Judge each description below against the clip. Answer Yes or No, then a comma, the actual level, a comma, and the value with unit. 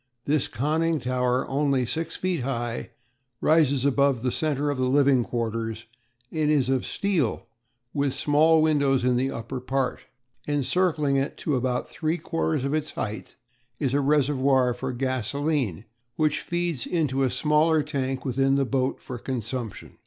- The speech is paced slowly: No, average, 155 wpm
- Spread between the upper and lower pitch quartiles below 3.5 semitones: Yes, average, 3.0 semitones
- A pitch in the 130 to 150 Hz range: Yes, low, 135 Hz